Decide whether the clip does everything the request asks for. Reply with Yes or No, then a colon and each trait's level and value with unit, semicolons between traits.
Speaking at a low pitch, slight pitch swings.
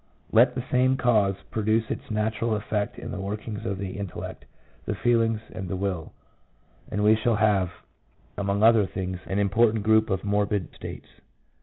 Yes: low, 105 Hz; narrow, 2.2 semitones